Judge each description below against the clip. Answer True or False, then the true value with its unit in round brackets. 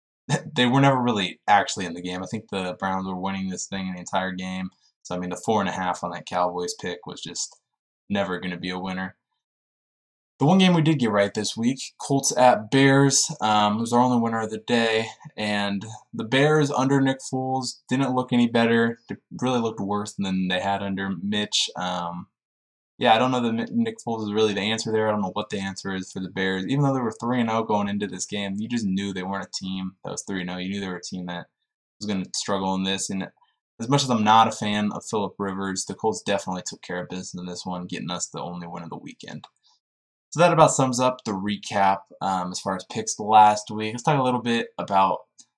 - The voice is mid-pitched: False (105 Hz)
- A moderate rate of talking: False (250 wpm)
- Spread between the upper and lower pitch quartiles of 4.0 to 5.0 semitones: True (4.3 semitones)